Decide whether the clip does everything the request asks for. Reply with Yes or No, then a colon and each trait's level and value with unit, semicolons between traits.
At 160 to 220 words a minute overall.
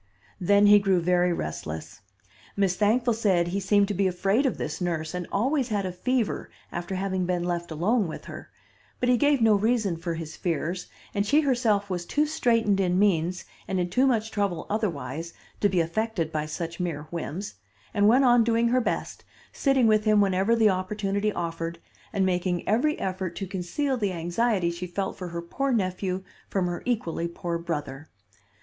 Yes: average, 185 wpm